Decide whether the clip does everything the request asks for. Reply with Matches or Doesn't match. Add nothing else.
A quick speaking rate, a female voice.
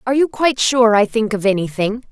Matches